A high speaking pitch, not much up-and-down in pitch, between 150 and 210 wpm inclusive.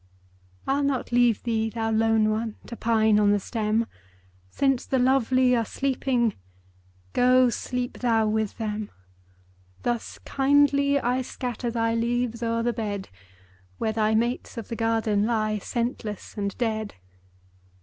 No: high, 230 Hz; narrow, 2.3 semitones; average, 140 wpm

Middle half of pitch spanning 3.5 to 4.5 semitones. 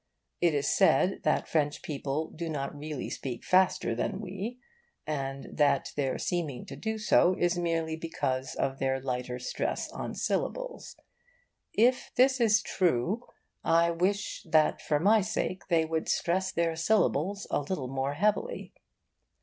No: wide, 5.4 semitones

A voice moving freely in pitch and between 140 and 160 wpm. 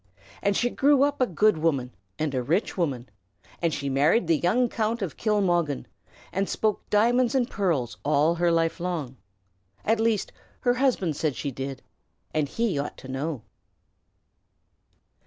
Yes: wide, 7.3 semitones; average, 155 wpm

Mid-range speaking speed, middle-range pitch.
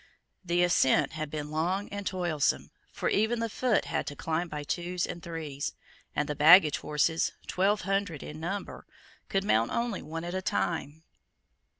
Yes: average, 170 wpm; medium, 170 Hz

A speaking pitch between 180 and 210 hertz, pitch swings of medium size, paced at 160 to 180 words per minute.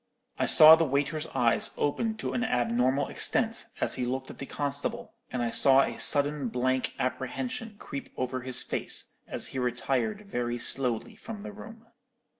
No: low, 135 Hz; average, 4.7 semitones; average, 170 wpm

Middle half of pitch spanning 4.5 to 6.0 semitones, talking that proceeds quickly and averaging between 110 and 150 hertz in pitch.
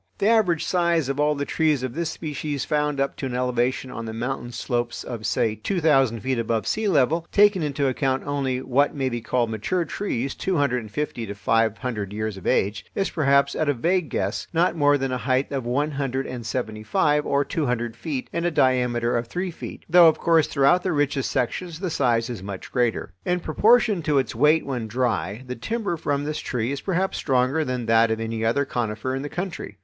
Yes: average, 4.8 semitones; fast, 220 wpm; low, 135 Hz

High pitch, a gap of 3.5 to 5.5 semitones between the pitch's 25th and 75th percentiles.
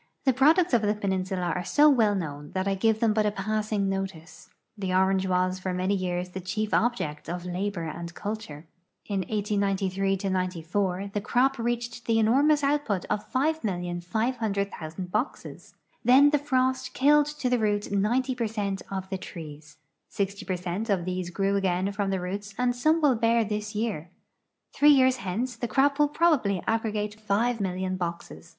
Yes: high, 200 Hz; average, 4.4 semitones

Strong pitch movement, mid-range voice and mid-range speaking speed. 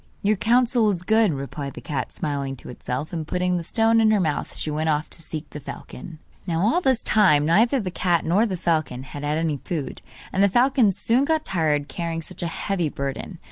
No: wide, 6.2 semitones; medium, 170 Hz; fast, 220 wpm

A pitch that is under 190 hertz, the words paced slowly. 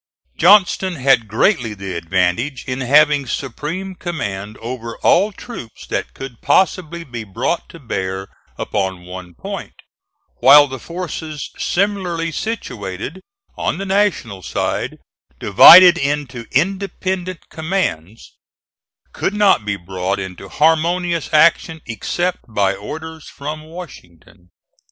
Yes: medium, 140 Hz; slow, 115 wpm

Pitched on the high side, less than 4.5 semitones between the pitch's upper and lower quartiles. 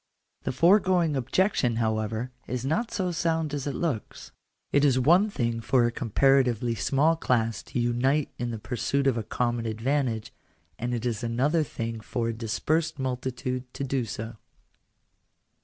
No: low, 125 Hz; average, 4.0 semitones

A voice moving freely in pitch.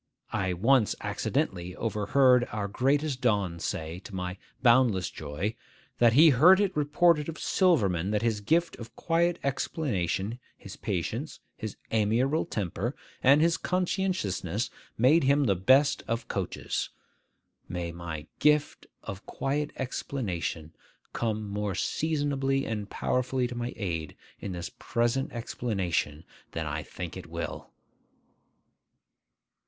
Yes: wide, 6.6 semitones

